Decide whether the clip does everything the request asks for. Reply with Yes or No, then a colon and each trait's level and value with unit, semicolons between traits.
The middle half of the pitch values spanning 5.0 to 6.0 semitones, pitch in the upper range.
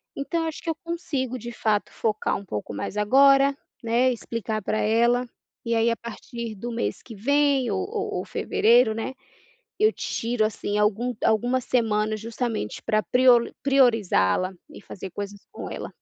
No: average, 3.2 semitones; high, 235 Hz